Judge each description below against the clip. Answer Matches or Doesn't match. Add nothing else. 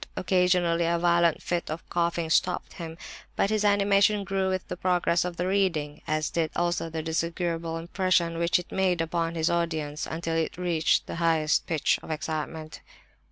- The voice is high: Doesn't match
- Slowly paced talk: Doesn't match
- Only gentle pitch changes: Matches